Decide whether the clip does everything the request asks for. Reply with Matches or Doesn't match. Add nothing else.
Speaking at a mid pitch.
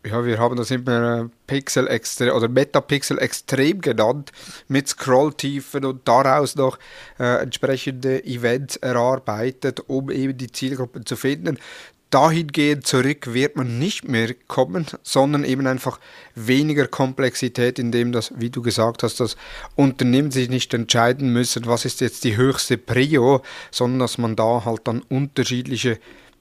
Doesn't match